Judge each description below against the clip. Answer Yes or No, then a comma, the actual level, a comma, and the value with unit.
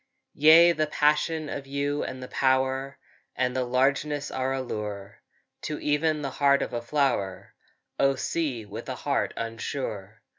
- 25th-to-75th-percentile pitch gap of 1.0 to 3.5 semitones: Yes, average, 2.9 semitones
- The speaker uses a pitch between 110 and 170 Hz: Yes, low, 135 Hz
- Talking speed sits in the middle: Yes, average, 155 wpm